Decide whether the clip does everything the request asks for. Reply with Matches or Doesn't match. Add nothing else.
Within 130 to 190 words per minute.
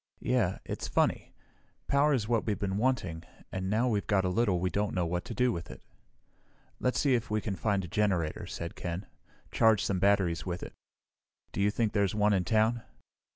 Doesn't match